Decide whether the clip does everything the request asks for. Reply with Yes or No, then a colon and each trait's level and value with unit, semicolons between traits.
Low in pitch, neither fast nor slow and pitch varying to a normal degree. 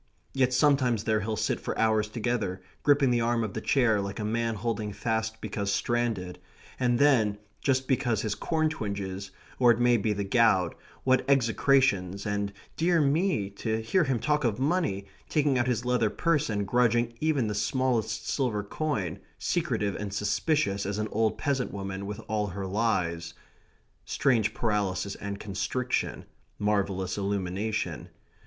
Yes: low, 110 Hz; average, 160 wpm; average, 4.0 semitones